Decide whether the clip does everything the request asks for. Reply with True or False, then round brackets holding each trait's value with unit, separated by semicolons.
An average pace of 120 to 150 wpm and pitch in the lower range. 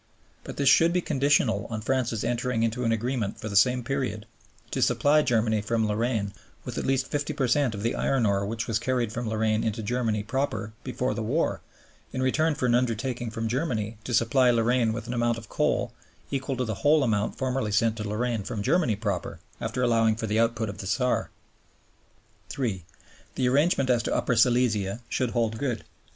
False (195 wpm; 115 Hz)